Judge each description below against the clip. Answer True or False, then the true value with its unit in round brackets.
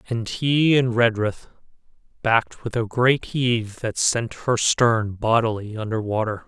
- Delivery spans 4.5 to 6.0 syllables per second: False (4.2 syllables/s)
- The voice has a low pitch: True (115 Hz)